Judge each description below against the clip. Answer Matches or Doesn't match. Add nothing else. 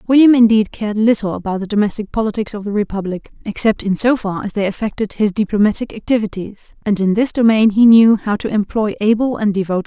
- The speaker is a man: Doesn't match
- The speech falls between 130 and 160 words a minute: Doesn't match